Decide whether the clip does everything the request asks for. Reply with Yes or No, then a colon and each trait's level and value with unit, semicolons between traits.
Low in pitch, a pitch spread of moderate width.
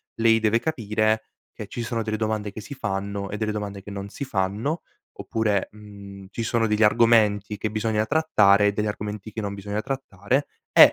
No: low, 105 Hz; narrow, 1.8 semitones